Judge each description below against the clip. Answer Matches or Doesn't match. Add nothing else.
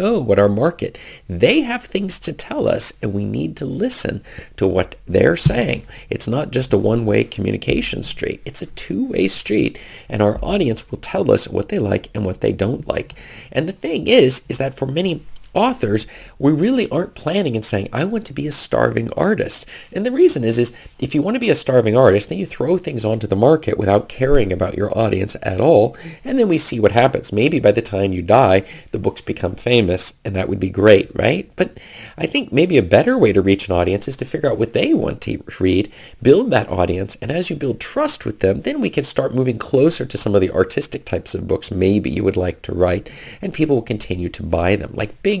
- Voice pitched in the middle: Doesn't match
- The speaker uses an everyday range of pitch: Doesn't match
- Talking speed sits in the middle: Doesn't match